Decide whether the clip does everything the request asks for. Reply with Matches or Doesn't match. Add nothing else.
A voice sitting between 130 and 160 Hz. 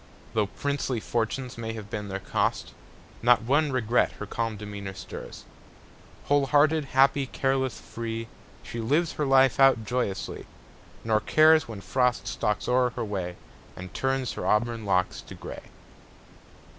Doesn't match